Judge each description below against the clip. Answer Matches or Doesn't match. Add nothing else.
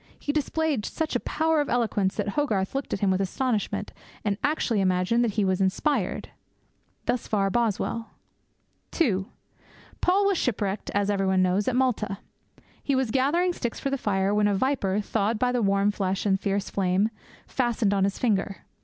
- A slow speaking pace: Doesn't match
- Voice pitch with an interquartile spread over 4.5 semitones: Matches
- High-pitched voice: Matches